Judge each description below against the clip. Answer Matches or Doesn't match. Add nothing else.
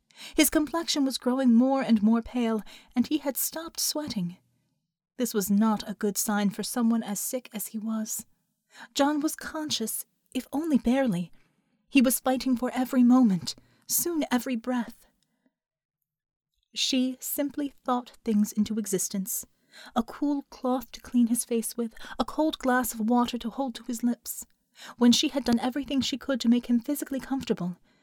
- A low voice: Doesn't match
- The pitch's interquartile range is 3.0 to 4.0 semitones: Matches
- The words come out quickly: Doesn't match